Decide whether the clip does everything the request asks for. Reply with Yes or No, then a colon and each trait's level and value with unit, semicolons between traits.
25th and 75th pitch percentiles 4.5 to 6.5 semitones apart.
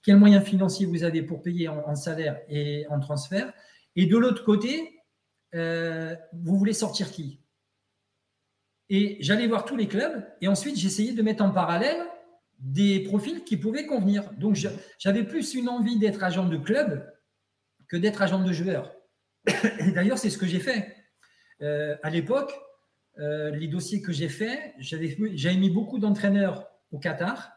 Yes: average, 4.9 semitones